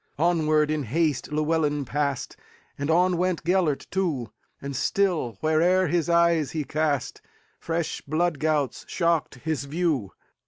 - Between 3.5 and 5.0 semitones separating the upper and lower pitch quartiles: No, average, 2.7 semitones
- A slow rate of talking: Yes, slow, 115 wpm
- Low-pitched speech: No, medium, 155 Hz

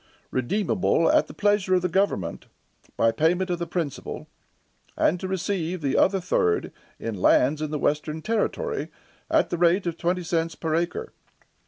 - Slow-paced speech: No, average, 165 wpm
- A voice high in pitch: No, medium, 175 Hz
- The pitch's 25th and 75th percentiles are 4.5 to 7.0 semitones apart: No, average, 3.5 semitones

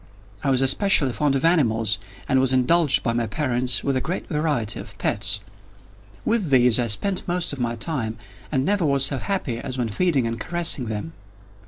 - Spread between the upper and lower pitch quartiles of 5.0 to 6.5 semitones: Yes, wide, 5.5 semitones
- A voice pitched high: No, low, 130 Hz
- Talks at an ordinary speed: Yes, average, 190 wpm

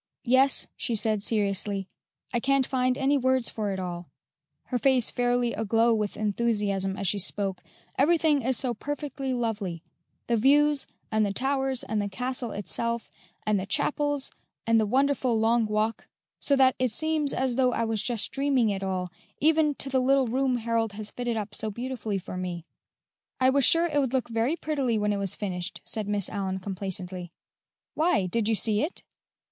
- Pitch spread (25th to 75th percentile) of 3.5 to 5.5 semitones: Yes, average, 4.5 semitones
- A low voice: No, high, 230 Hz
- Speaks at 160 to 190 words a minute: Yes, average, 180 wpm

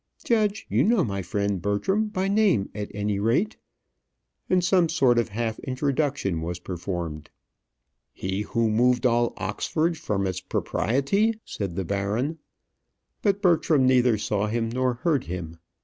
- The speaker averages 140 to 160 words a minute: Yes, average, 145 wpm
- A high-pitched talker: No, low, 120 Hz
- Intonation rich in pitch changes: Yes, wide, 8.3 semitones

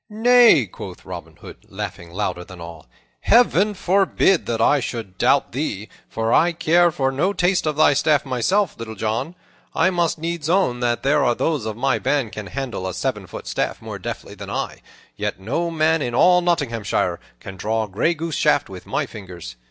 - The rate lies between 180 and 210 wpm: Yes, average, 190 wpm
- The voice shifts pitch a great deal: Yes, wide, 7.6 semitones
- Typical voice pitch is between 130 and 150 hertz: Yes, medium, 140 Hz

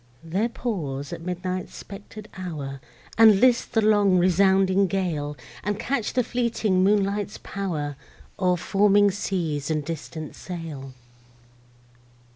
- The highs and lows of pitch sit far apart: No, average, 4.1 semitones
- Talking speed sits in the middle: No, slow, 115 wpm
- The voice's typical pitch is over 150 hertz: Yes, medium, 185 Hz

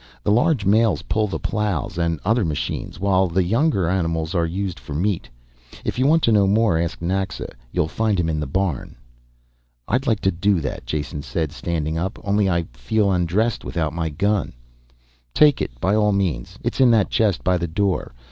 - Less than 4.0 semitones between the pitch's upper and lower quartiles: No, average, 4.4 semitones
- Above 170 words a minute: Yes, average, 195 wpm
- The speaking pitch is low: Yes, very low, 95 Hz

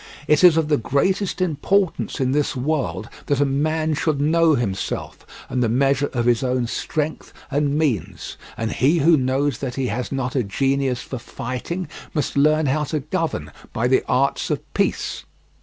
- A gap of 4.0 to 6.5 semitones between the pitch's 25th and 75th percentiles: No, average, 3.5 semitones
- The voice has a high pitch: No, medium, 140 Hz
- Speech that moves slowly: No, average, 175 wpm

